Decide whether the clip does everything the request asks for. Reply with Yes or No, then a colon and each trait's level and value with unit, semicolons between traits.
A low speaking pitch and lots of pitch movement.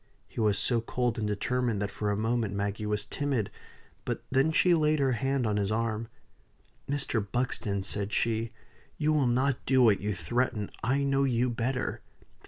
No: low, 115 Hz; average, 3.8 semitones